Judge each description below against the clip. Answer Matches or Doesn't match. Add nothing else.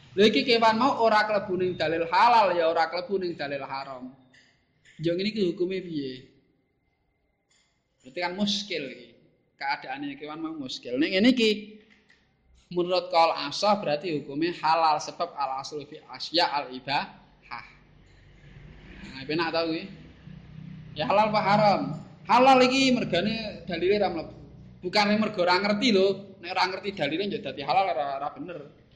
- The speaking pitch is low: Doesn't match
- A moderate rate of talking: Doesn't match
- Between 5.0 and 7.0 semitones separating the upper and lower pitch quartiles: Matches